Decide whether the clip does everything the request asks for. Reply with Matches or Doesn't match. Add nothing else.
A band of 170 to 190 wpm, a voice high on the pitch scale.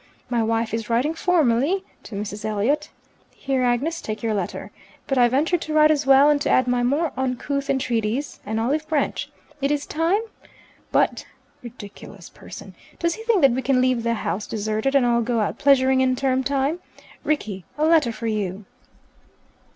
Matches